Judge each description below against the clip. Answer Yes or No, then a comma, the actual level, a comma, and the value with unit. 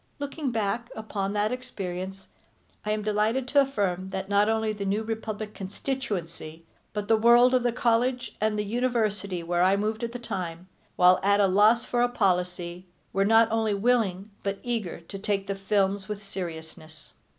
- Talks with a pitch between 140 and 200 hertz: No, high, 210 Hz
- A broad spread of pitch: No, average, 3.1 semitones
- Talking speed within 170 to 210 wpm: Yes, average, 175 wpm